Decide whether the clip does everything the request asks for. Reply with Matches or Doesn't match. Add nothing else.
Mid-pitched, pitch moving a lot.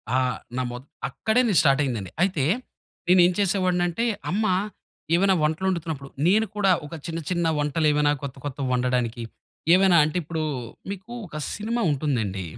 Matches